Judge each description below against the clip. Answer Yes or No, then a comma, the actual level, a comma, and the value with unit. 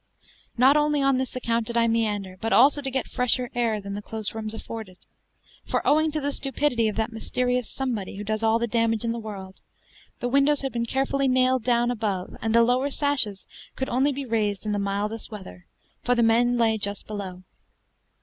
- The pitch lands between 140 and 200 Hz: No, high, 230 Hz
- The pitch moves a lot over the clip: No, average, 3.3 semitones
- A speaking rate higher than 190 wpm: Yes, fast, 205 wpm